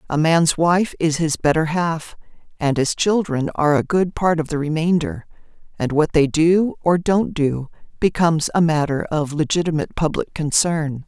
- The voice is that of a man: No, female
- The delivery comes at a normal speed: Yes, average, 170 wpm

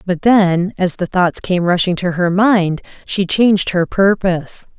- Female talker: Yes, female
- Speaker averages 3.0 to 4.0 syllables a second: No, 4.2 syllables/s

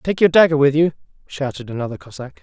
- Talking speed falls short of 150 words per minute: No, average, 200 wpm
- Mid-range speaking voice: Yes, medium, 145 Hz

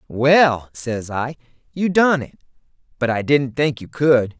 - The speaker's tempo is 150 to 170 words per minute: Yes, average, 165 wpm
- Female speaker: No, male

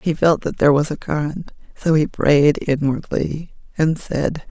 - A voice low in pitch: No, medium, 150 Hz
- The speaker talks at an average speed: Yes, average, 175 wpm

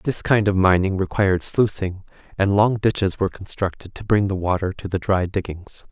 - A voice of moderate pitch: No, very low, 95 Hz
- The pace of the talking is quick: No, average, 195 wpm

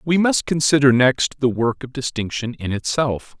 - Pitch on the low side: Yes, low, 130 Hz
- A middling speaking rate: Yes, average, 175 wpm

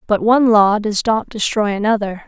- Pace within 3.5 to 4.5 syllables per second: No, 5.3 syllables/s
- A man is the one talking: No, female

